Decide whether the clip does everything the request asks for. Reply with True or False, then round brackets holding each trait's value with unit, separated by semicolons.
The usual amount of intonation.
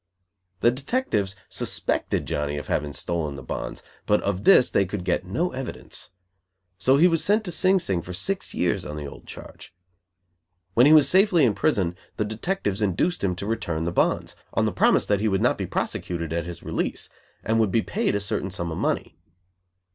False (9.0 semitones)